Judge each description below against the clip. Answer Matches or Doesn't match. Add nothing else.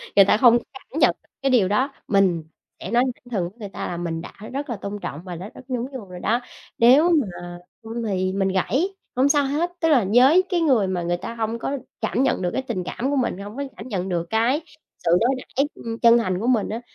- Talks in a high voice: Matches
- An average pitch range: Doesn't match